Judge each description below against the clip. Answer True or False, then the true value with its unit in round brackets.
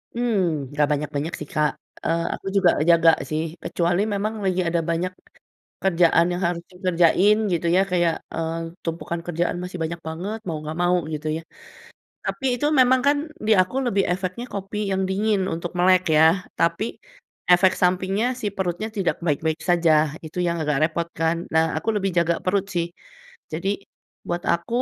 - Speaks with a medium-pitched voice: True (175 Hz)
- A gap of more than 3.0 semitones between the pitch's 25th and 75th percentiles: False (2.6 semitones)